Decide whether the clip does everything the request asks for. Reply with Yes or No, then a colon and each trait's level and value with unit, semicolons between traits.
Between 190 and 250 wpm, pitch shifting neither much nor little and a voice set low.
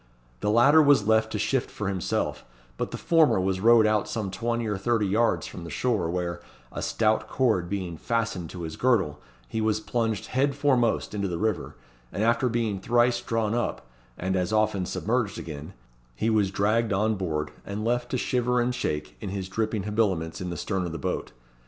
Yes: average, 195 wpm; average, 3.9 semitones; low, 110 Hz